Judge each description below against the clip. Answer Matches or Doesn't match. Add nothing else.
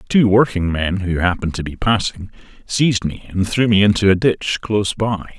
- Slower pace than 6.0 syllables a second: Matches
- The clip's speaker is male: Matches